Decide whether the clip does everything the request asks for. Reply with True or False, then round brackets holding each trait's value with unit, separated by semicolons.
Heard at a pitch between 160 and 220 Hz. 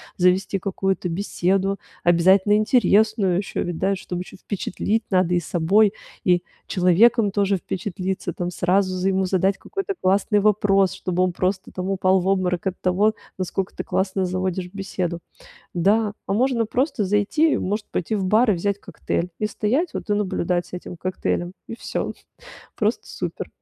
True (190 Hz)